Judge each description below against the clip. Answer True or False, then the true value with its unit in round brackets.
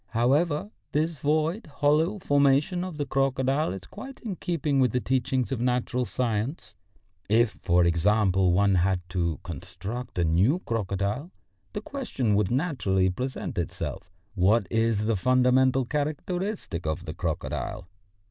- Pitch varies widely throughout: True (7.0 semitones)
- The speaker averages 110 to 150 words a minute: True (140 wpm)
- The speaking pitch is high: False (125 Hz)